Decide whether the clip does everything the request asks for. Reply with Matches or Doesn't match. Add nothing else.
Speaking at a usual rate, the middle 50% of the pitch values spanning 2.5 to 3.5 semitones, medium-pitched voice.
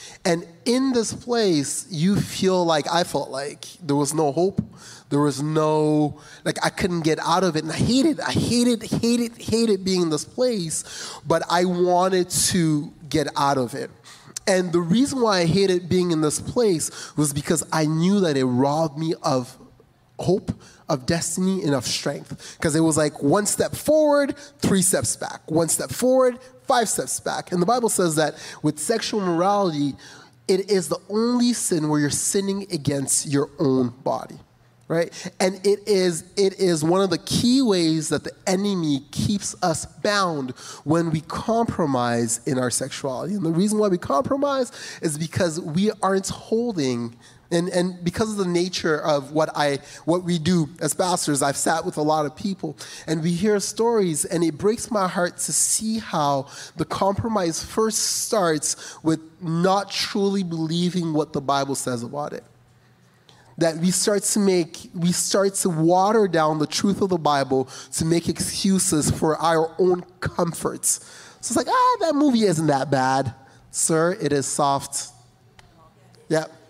Doesn't match